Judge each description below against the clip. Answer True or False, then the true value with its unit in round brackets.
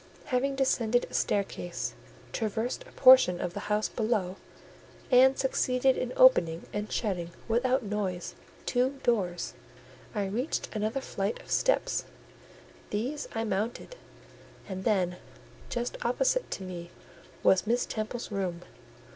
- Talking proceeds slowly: True (125 wpm)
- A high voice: True (220 Hz)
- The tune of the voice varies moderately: True (4.8 semitones)